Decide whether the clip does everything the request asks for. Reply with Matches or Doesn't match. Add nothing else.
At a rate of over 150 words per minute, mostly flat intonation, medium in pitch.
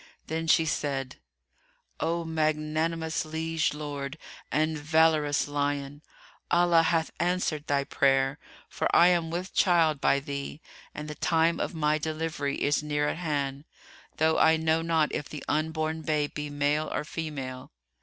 Doesn't match